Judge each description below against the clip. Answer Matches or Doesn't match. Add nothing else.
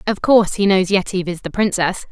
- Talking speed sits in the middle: Doesn't match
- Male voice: Doesn't match